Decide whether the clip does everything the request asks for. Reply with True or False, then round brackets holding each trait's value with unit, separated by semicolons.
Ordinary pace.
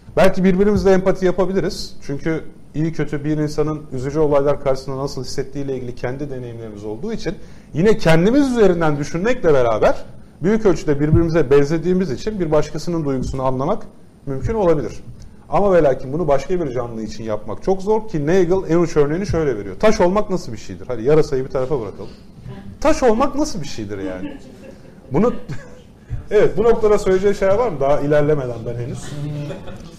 False (160 wpm)